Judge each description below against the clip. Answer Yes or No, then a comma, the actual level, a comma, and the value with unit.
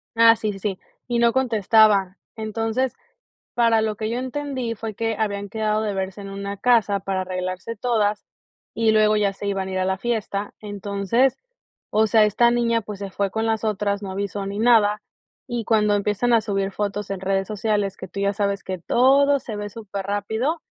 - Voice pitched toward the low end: No, high, 210 Hz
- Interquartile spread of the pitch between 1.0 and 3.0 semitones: Yes, narrow, 2.4 semitones